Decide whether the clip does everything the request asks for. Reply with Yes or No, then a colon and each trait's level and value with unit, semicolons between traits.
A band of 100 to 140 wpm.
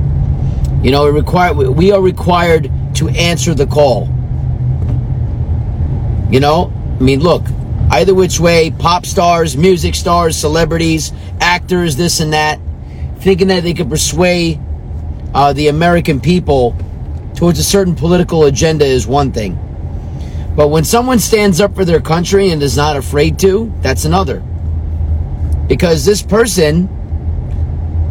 Yes: slow, 135 wpm